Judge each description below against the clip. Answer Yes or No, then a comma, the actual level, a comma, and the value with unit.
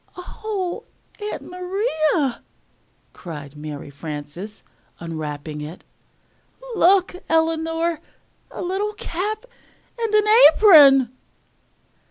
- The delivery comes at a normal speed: No, slow, 75 wpm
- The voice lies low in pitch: No, very high, 320 Hz